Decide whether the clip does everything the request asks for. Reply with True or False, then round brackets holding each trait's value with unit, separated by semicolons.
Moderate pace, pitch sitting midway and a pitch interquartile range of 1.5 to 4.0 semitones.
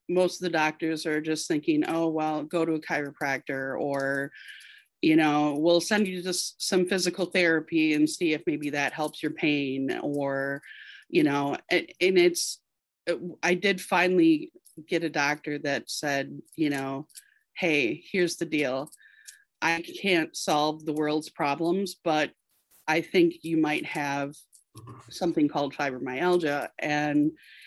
True (145 wpm; 155 Hz; 3.5 semitones)